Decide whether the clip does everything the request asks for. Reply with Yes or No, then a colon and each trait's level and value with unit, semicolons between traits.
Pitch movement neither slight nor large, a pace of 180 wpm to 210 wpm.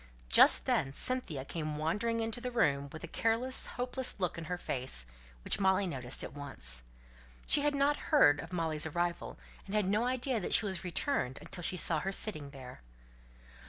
No: wide, 7.8 semitones; average, 185 wpm